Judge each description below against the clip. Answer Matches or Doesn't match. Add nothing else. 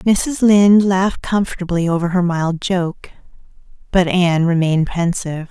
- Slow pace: Matches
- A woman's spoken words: Matches